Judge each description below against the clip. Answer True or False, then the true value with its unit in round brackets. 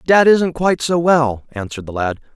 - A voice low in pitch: False (145 Hz)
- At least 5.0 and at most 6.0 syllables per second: True (5.3 syllables/s)